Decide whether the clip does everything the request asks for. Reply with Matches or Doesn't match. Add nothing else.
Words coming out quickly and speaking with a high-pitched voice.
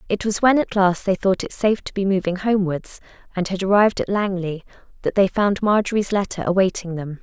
Matches